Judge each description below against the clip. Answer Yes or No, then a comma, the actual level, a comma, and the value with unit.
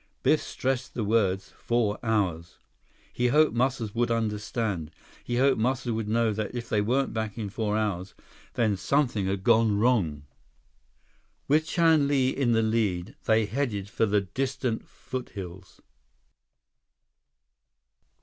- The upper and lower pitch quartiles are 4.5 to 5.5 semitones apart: No, average, 3.4 semitones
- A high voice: No, low, 110 Hz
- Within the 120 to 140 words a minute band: Yes, slow, 135 wpm